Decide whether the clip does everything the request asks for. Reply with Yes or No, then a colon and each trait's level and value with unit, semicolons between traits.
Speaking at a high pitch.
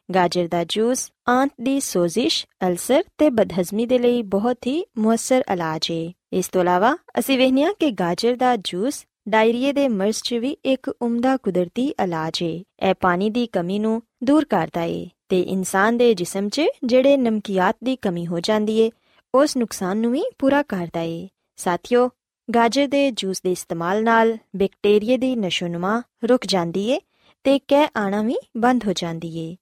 Yes: high, 225 Hz